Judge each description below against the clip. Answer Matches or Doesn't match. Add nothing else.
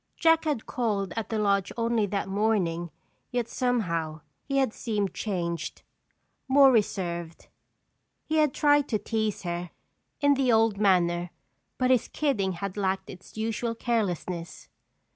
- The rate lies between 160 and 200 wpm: Doesn't match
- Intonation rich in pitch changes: Doesn't match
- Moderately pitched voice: Doesn't match